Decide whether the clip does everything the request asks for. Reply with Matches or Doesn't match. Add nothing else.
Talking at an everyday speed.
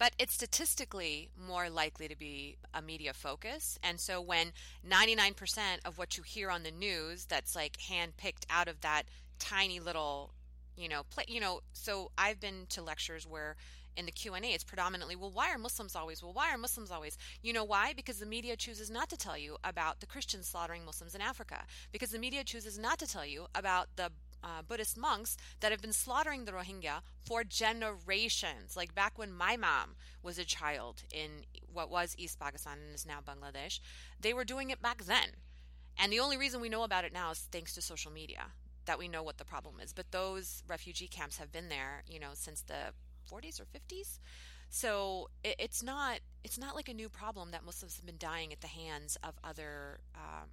Doesn't match